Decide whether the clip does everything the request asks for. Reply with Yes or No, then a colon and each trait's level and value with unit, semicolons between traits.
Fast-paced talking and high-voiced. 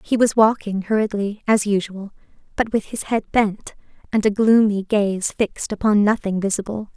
No: average, 165 wpm; high, 210 Hz